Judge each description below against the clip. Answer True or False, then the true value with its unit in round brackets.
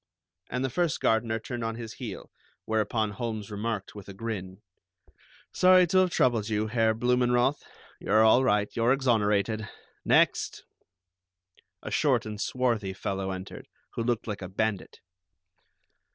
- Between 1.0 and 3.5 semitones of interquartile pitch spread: True (2.8 semitones)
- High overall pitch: False (110 Hz)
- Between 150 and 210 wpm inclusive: False (140 wpm)